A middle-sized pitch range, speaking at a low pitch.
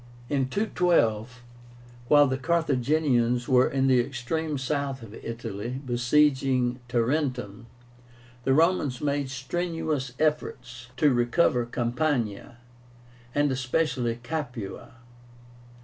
Yes: average, 3.6 semitones; low, 130 Hz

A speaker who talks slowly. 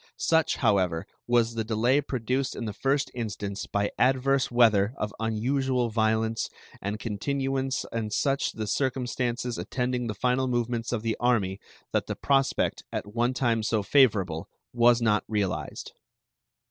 No: average, 145 wpm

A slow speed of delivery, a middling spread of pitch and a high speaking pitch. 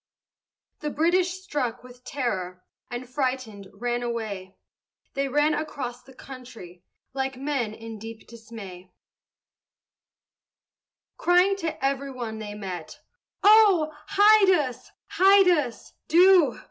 No: slow, 110 wpm; wide, 5.8 semitones; very high, 255 Hz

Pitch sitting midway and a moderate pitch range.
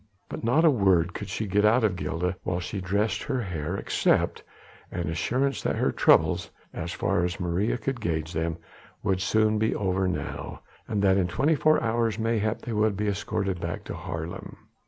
No: low, 100 Hz; average, 3.8 semitones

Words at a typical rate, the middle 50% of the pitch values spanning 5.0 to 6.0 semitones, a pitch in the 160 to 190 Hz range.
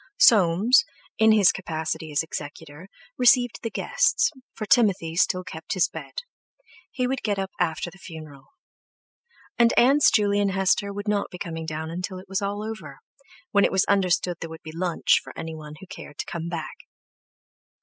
No: average, 170 wpm; average, 4.5 semitones; medium, 185 Hz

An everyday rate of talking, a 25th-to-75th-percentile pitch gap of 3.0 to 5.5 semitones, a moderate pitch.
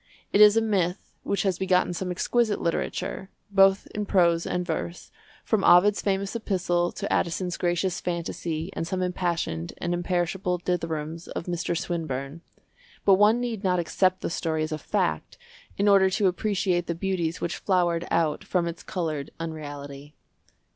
No: average, 160 wpm; narrow, 2.5 semitones; medium, 175 Hz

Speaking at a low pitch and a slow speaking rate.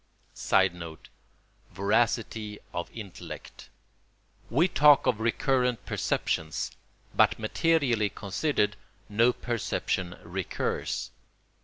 Yes: low, 110 Hz; slow, 75 wpm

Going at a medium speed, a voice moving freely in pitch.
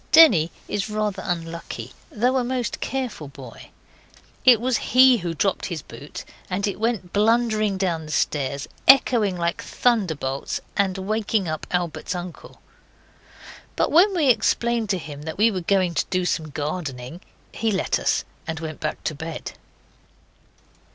Yes: average, 150 wpm; wide, 5.9 semitones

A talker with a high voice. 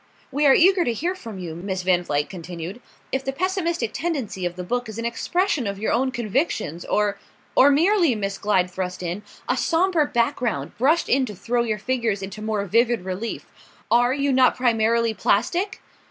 Yes: high, 230 Hz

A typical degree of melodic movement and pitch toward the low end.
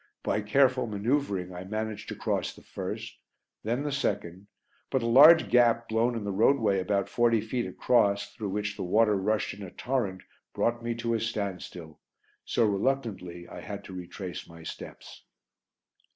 Yes: average, 3.5 semitones; low, 110 Hz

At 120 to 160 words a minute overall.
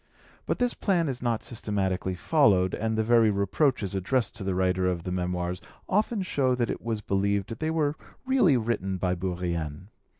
No: average, 175 wpm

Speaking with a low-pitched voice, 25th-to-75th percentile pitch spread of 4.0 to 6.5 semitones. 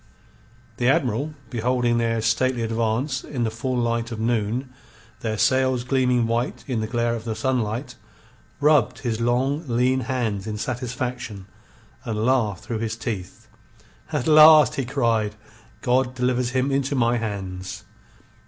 No: low, 120 Hz; narrow, 2.5 semitones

